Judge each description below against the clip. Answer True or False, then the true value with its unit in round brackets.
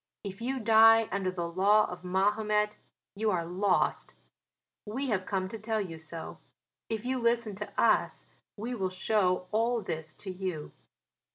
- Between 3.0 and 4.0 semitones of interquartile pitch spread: True (3.3 semitones)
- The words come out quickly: False (160 wpm)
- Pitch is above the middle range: True (205 Hz)